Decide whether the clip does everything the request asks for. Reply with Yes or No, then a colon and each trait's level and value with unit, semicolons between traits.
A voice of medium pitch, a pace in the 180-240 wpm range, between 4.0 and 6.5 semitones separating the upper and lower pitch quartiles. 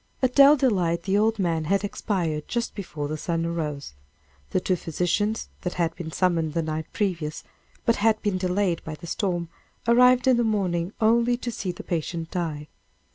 Yes: medium, 180 Hz; average, 185 wpm; average, 4.7 semitones